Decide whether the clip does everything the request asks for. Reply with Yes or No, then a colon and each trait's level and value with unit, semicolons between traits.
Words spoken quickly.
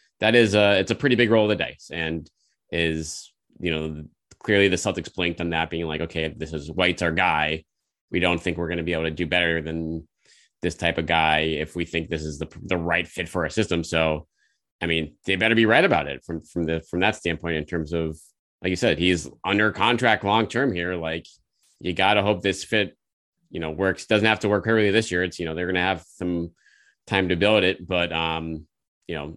Yes: fast, 240 wpm